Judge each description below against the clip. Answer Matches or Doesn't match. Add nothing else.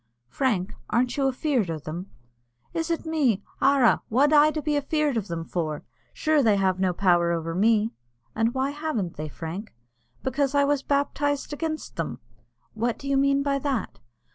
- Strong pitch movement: Matches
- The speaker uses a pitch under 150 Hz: Doesn't match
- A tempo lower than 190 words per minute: Matches